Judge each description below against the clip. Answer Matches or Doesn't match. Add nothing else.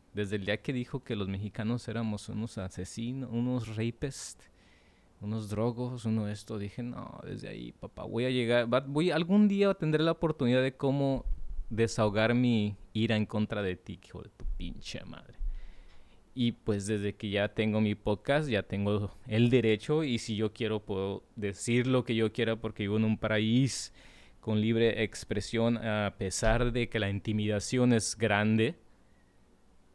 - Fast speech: Doesn't match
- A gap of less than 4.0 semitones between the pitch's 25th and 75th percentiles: Matches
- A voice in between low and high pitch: Doesn't match